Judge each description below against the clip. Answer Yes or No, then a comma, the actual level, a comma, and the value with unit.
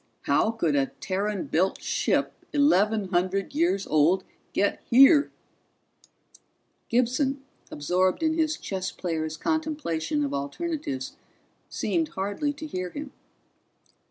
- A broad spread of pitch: Yes, wide, 8.8 semitones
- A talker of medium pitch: No, high, 200 Hz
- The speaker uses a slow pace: Yes, slow, 110 wpm